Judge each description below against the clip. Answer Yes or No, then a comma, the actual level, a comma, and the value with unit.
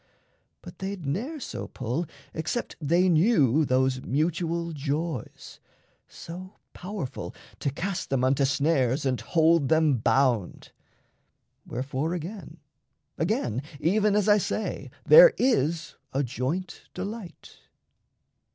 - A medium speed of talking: No, slow, 110 wpm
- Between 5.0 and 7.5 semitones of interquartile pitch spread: Yes, wide, 5.6 semitones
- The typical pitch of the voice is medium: Yes, medium, 160 Hz